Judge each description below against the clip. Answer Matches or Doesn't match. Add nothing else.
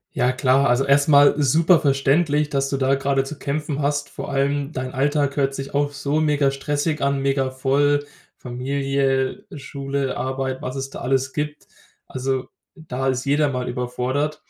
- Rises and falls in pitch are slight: Matches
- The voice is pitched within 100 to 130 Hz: Doesn't match